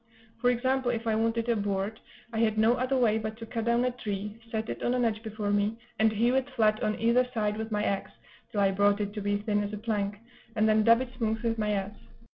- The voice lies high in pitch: Yes, high, 220 Hz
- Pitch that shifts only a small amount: Yes, narrow, 2.0 semitones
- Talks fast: Yes, fast, 260 wpm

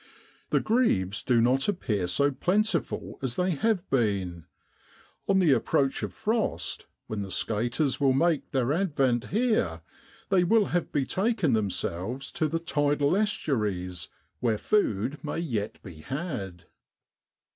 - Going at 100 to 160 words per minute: Yes, slow, 135 wpm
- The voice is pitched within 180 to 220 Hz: No, low, 135 Hz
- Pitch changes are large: Yes, wide, 8.8 semitones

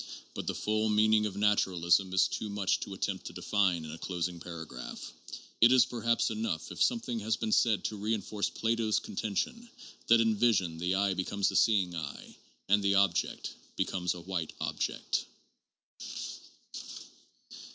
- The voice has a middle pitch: No, low, 100 Hz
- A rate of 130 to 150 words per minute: No, average, 160 wpm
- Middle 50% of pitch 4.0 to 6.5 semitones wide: No, average, 3.3 semitones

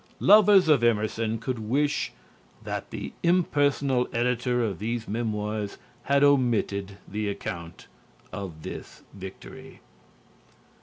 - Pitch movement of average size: Yes, average, 5.0 semitones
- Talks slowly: Yes, slow, 105 wpm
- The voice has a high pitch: No, low, 115 Hz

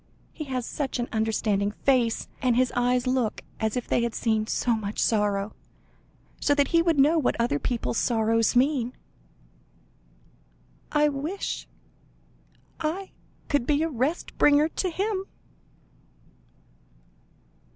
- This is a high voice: Yes, very high, 250 Hz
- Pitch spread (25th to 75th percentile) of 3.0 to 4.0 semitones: No, average, 4.7 semitones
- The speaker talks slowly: Yes, slow, 130 wpm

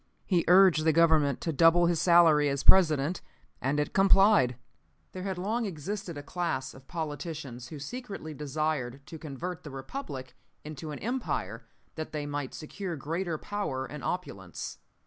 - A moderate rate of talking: Yes, average, 155 wpm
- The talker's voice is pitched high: No, medium, 155 Hz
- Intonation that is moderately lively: Yes, average, 4.3 semitones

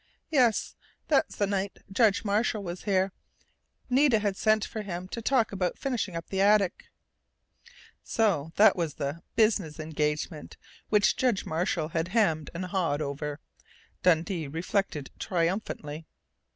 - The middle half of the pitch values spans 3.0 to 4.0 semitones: No, average, 4.7 semitones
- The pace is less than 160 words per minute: Yes, average, 140 wpm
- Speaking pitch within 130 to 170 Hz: No, high, 190 Hz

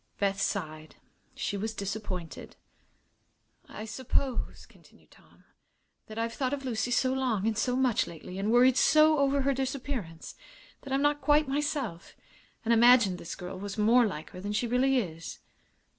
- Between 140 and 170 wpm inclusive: Yes, average, 160 wpm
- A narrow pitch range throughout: No, average, 5.1 semitones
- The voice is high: Yes, high, 230 Hz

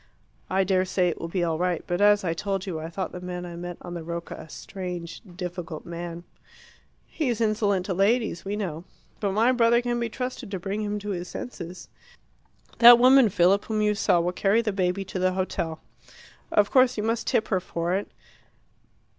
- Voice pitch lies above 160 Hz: Yes, high, 190 Hz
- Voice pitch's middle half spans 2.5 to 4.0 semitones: Yes, average, 3.3 semitones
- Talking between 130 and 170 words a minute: No, fast, 205 wpm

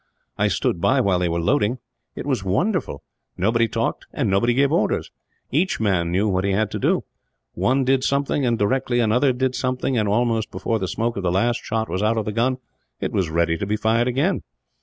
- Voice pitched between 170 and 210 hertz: No, low, 115 Hz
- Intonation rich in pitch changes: No, average, 4.5 semitones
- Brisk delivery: Yes, fast, 215 wpm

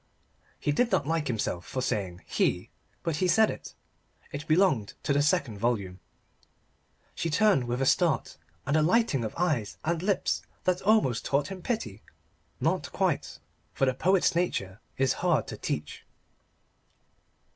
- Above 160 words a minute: No, average, 155 wpm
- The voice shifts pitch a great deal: Yes, wide, 7.3 semitones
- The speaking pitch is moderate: Yes, medium, 145 Hz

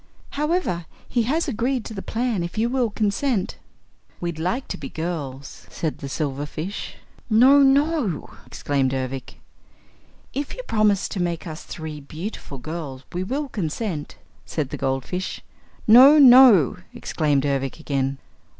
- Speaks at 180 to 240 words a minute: No, average, 140 wpm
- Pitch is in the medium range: Yes, medium, 180 Hz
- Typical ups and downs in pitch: No, wide, 8.9 semitones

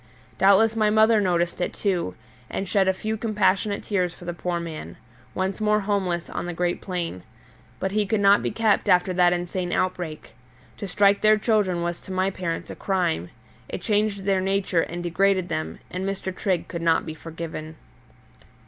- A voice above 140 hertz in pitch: Yes, medium, 185 Hz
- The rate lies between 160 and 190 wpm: Yes, average, 185 wpm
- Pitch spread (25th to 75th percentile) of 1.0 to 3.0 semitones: Yes, narrow, 2.6 semitones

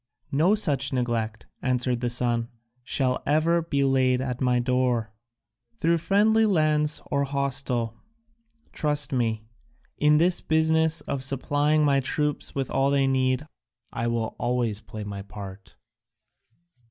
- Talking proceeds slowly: Yes, slow, 130 wpm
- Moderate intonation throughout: Yes, average, 3.8 semitones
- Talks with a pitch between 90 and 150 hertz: Yes, low, 135 Hz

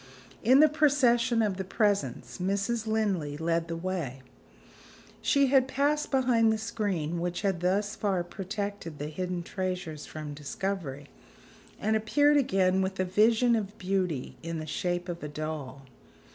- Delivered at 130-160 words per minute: Yes, average, 150 wpm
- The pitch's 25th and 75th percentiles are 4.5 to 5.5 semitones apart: Yes, average, 4.8 semitones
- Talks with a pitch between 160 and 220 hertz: Yes, high, 190 Hz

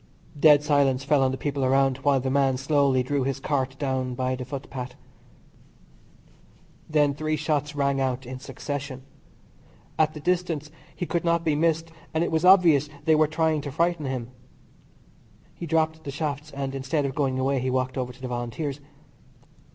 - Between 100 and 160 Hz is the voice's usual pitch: Yes, medium, 140 Hz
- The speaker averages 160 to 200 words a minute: Yes, average, 175 wpm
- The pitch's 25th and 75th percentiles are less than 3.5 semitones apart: Yes, average, 2.8 semitones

